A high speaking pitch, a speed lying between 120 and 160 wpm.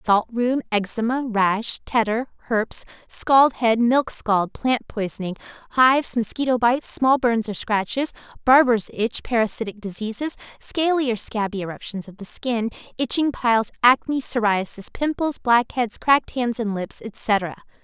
Yes: high, 235 Hz; average, 140 wpm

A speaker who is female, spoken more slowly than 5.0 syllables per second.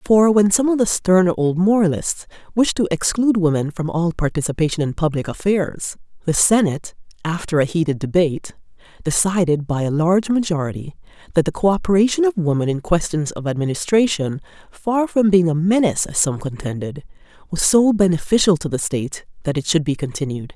No: female; 5.6 syllables/s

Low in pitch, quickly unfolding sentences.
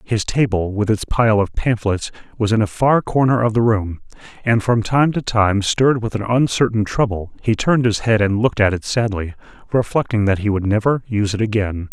Yes: low, 110 Hz; fast, 210 wpm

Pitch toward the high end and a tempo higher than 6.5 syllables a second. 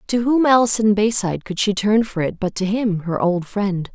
No: high, 205 Hz; 5.0 syllables/s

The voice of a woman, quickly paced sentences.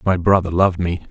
No: male; fast, 215 wpm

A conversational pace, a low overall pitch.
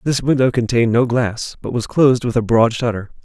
No: fast, 220 wpm; low, 120 Hz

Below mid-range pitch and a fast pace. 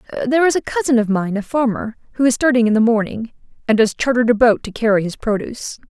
No: high, 235 Hz; fast, 235 wpm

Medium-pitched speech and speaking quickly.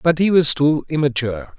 No: medium, 145 Hz; average, 190 wpm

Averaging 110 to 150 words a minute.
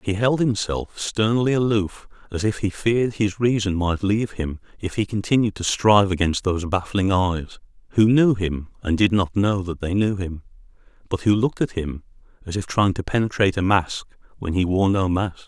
No: average, 200 wpm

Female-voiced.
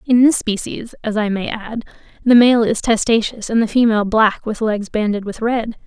Yes: female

